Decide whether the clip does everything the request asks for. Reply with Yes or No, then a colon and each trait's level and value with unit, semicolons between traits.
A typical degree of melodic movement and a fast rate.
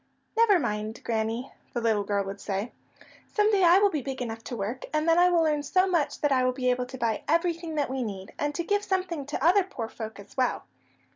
No: wide, 7.1 semitones; fast, 240 wpm